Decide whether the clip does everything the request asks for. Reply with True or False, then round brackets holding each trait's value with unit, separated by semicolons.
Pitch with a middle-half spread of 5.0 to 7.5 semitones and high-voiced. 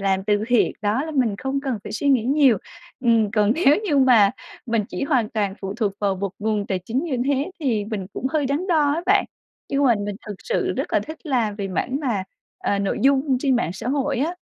True (5.3 semitones; 245 Hz)